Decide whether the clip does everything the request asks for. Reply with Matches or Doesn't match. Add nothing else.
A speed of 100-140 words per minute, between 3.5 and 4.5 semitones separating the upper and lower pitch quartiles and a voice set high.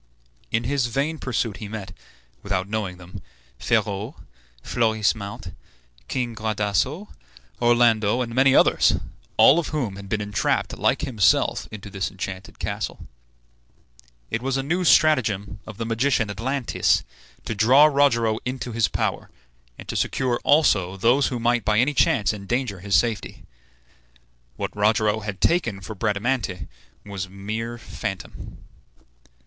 Doesn't match